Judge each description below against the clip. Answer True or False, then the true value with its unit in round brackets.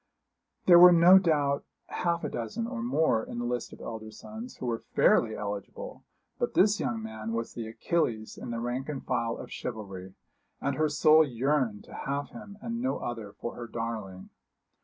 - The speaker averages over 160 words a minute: True (185 wpm)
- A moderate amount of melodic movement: False (7.1 semitones)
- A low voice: True (120 Hz)